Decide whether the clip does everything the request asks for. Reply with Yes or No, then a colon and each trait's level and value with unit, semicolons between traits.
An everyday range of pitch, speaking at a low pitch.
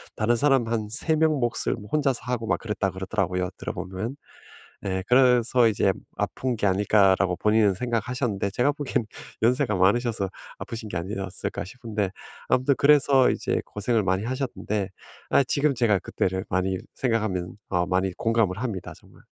Yes: average, 4.6 semitones; low, 110 Hz